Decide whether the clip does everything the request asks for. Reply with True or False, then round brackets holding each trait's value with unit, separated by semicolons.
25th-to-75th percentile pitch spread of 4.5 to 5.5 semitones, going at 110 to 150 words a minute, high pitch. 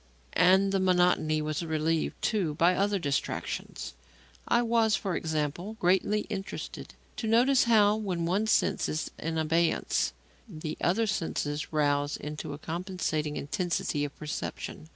False (4.8 semitones; 135 wpm; 175 Hz)